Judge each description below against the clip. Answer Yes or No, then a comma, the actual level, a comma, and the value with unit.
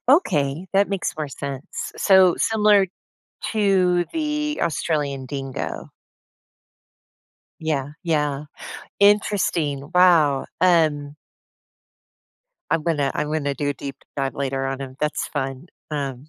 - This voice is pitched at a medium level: Yes, medium, 150 Hz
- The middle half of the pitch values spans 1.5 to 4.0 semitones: No, average, 4.9 semitones